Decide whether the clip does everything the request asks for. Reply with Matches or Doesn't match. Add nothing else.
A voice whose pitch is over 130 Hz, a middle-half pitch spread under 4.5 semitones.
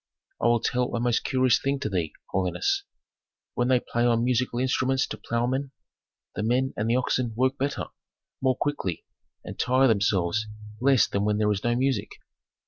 Doesn't match